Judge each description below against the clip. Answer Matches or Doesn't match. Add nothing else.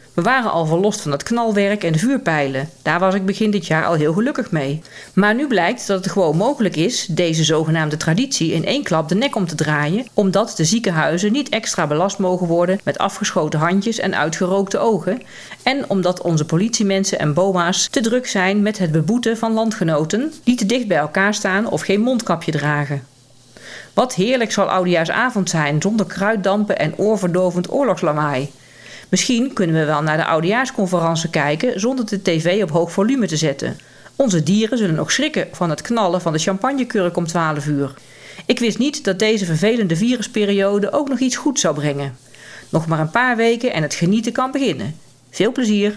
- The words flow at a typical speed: Matches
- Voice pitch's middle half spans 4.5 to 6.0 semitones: Matches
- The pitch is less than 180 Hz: Doesn't match